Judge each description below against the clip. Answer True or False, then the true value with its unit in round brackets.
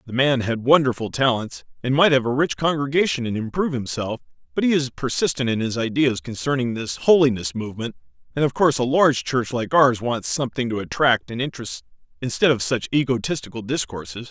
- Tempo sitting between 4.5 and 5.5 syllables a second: False (5.9 syllables/s)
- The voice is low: True (125 Hz)